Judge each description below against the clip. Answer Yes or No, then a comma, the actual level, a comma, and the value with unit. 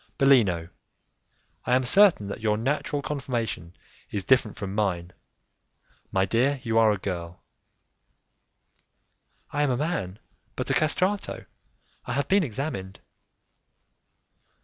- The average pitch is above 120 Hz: No, low, 115 Hz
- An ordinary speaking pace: No, slow, 120 wpm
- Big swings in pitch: Yes, wide, 6.6 semitones